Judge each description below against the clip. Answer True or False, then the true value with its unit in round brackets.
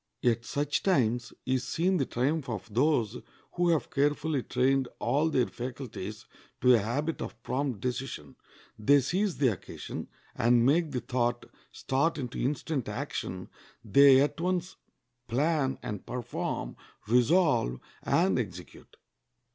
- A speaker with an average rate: False (130 wpm)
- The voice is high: False (130 Hz)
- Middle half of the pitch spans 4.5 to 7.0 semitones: False (4.0 semitones)